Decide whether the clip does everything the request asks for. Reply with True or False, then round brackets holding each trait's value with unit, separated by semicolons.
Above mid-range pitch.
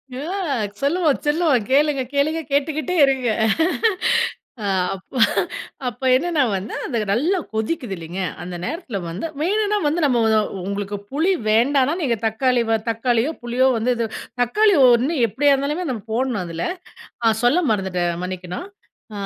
True (255 Hz)